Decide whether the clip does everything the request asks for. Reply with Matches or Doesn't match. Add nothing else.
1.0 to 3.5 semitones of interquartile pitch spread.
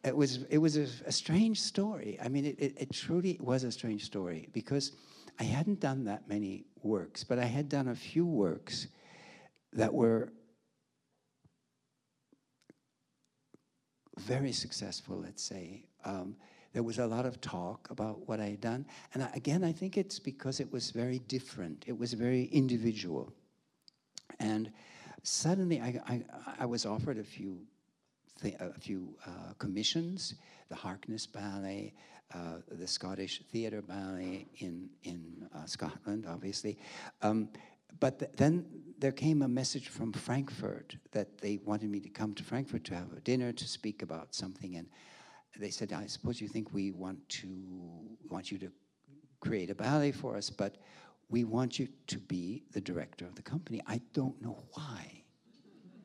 Doesn't match